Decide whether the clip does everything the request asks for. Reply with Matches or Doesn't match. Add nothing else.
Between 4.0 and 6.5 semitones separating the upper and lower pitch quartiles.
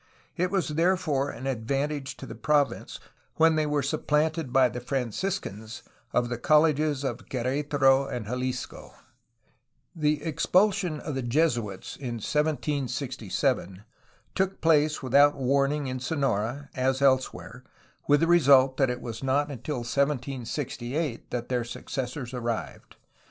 Doesn't match